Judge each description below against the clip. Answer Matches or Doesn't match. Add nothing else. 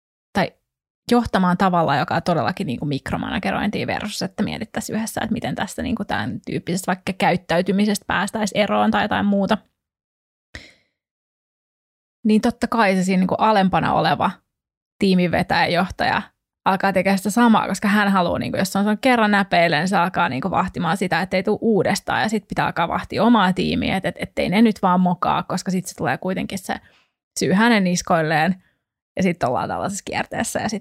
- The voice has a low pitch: Doesn't match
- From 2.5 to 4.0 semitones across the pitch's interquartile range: Matches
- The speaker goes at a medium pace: Doesn't match